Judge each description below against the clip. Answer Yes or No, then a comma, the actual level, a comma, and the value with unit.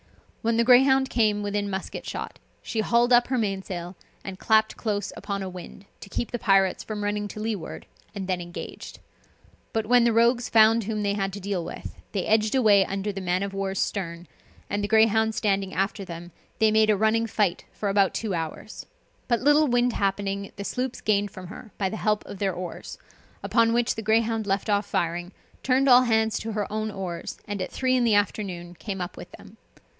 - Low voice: No, high, 205 Hz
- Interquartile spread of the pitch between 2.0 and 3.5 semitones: Yes, narrow, 2.6 semitones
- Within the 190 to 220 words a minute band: Yes, fast, 205 wpm